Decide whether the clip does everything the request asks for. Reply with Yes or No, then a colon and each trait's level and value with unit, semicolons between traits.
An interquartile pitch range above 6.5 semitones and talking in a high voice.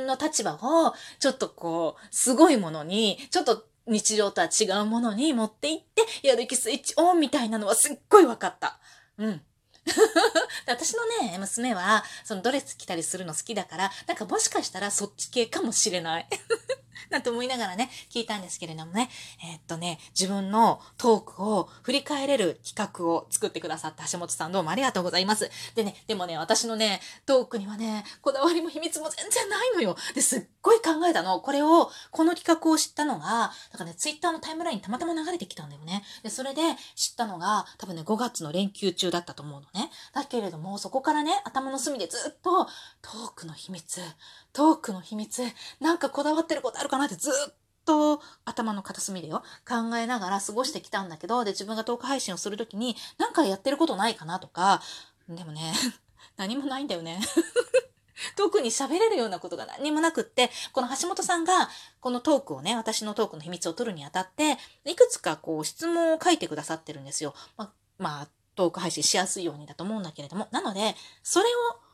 Yes: wide, 8.3 semitones; high, 230 Hz